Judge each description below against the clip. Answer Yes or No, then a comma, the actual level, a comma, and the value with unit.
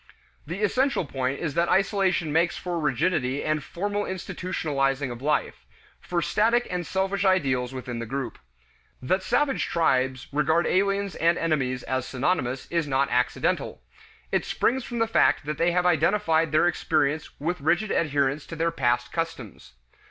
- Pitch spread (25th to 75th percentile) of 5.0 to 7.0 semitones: Yes, average, 5.3 semitones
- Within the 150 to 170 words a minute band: Yes, average, 155 wpm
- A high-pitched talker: No, medium, 160 Hz